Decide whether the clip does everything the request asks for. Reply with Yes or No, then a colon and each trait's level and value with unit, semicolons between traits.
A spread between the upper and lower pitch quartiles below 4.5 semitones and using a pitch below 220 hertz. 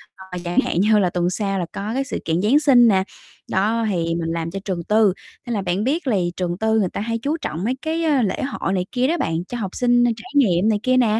No: average, 5.0 semitones; high, 210 Hz